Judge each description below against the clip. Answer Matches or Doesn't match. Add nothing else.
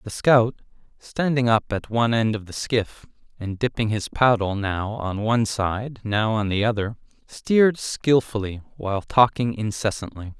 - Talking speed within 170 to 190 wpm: Doesn't match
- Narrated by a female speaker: Doesn't match